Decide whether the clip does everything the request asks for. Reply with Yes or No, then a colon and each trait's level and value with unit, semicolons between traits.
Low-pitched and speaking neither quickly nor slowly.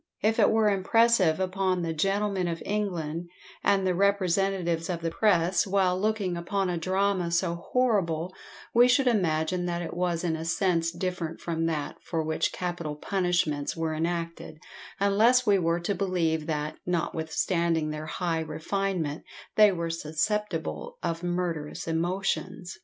No: medium, 175 Hz; average, 145 wpm